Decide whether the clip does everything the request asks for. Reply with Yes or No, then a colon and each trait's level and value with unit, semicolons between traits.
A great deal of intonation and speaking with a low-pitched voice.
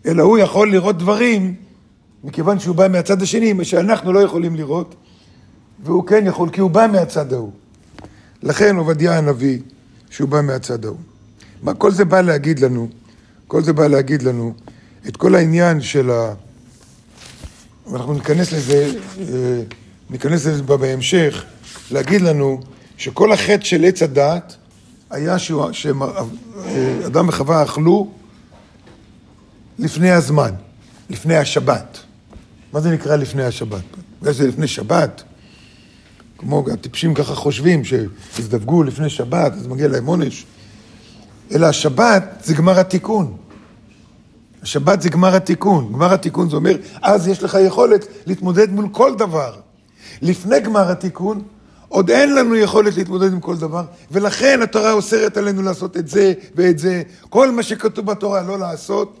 No: wide, 6.5 semitones; medium, 165 Hz